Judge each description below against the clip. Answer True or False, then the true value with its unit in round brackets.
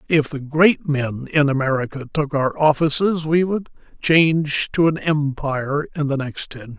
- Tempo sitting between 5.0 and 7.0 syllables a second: False (4.6 syllables/s)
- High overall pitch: False (145 Hz)